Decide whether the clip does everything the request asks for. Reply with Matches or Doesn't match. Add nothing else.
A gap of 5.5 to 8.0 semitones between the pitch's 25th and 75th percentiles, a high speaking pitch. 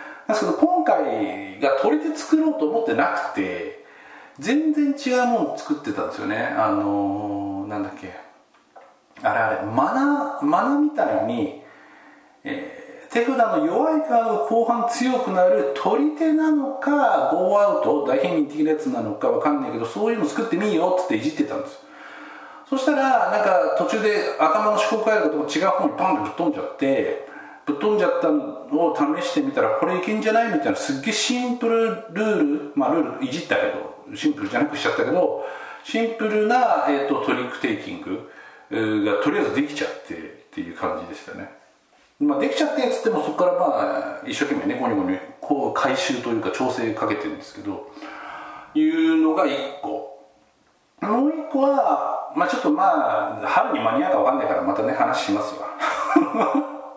Matches